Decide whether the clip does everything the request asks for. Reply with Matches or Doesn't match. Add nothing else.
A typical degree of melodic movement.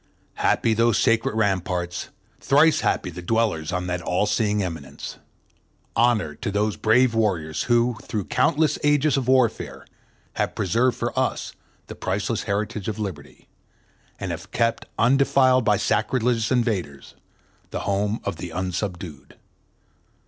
Matches